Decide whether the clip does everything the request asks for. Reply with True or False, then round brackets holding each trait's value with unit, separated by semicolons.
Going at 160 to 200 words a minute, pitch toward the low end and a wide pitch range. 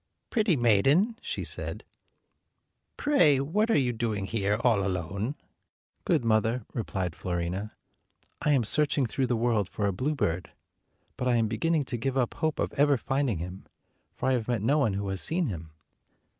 True (170 wpm; 120 Hz; 5.9 semitones)